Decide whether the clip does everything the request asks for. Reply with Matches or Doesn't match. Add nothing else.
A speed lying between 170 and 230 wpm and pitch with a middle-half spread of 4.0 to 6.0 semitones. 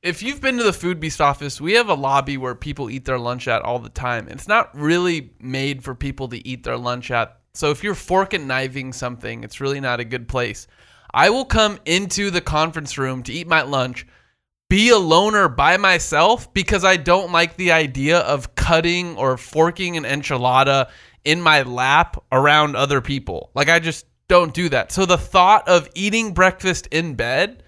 Matches